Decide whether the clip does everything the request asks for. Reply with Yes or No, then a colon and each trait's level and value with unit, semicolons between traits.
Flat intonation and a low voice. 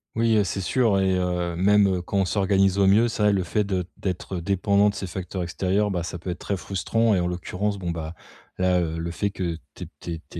Yes: narrow, 2.3 semitones; very low, 95 Hz